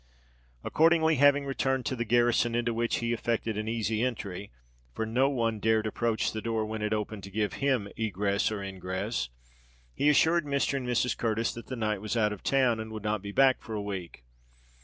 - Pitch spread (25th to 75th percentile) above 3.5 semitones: No, average, 3.1 semitones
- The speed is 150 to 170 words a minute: No, average, 195 wpm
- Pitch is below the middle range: Yes, low, 110 Hz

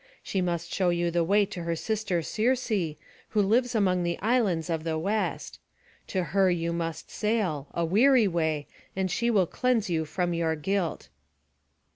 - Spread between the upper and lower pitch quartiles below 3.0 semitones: No, average, 4.0 semitones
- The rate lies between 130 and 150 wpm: No, average, 170 wpm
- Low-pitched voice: No, medium, 180 Hz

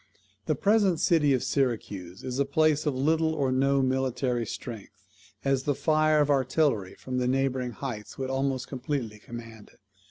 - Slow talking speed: No, average, 165 wpm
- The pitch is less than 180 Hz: Yes, low, 135 Hz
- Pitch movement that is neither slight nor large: Yes, average, 3.0 semitones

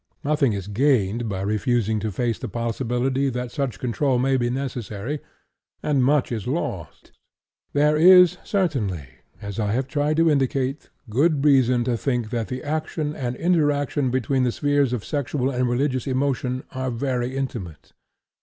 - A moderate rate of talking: Yes, average, 155 wpm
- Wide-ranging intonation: No, average, 3.4 semitones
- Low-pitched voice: Yes, low, 130 Hz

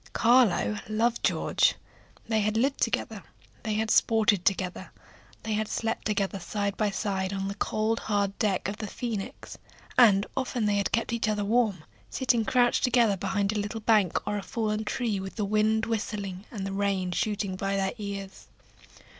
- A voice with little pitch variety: Yes, narrow, 2.2 semitones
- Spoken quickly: No, average, 175 wpm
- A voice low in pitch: No, high, 210 Hz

